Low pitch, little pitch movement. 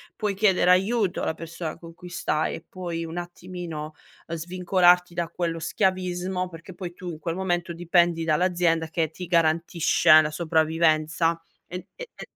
No: medium, 175 Hz; narrow, 1.7 semitones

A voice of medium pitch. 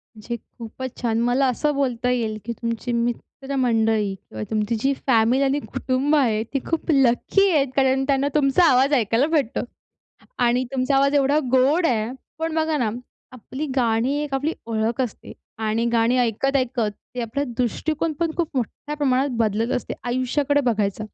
No: very high, 255 Hz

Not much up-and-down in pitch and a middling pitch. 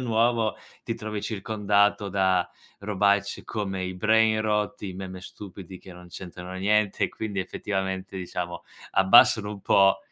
No: narrow, 2.2 semitones; low, 100 Hz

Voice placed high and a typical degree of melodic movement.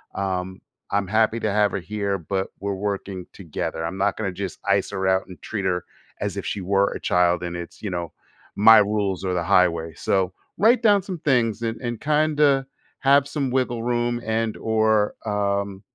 No: low, 100 Hz; average, 3.7 semitones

